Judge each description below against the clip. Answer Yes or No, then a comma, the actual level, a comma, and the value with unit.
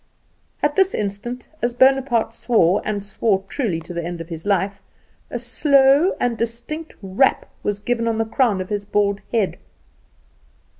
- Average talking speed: Yes, average, 160 wpm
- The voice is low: No, high, 225 Hz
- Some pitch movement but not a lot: Yes, average, 4.0 semitones